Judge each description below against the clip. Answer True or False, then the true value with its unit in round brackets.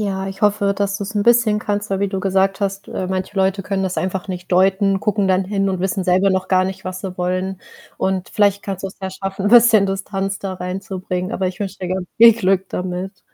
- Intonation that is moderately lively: False (1.3 semitones)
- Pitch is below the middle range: False (195 Hz)